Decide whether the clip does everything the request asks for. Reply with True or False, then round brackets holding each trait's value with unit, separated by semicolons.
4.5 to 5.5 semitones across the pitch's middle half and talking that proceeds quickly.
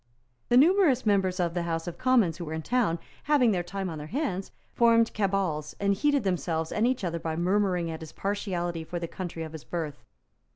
True (4.8 semitones; 210 wpm)